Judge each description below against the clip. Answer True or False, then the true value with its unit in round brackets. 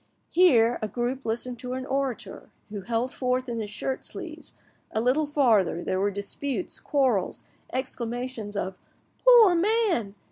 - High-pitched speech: True (250 Hz)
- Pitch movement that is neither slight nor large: True (4.0 semitones)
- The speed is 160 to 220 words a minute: False (145 wpm)